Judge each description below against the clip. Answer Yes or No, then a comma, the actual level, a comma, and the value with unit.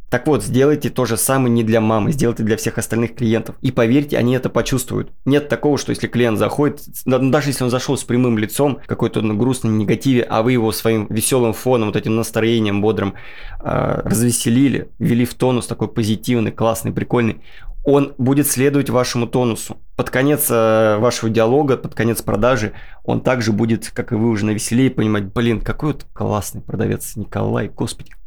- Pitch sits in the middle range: No, low, 115 Hz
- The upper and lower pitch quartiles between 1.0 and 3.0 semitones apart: Yes, narrow, 2.6 semitones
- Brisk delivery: Yes, fast, 175 wpm